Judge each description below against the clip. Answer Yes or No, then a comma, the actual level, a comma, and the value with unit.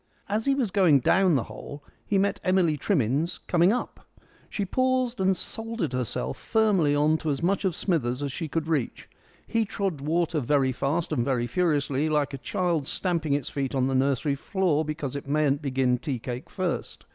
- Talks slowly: No, average, 190 wpm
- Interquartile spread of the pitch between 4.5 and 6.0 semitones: Yes, average, 5.3 semitones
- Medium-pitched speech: Yes, medium, 155 Hz